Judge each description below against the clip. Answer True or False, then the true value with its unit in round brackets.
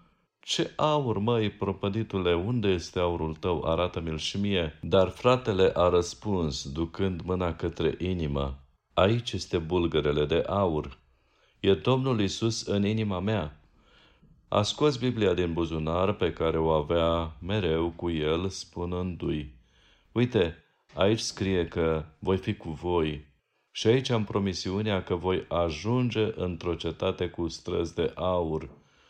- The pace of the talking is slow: False (130 wpm)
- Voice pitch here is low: True (90 Hz)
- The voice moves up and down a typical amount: True (4.0 semitones)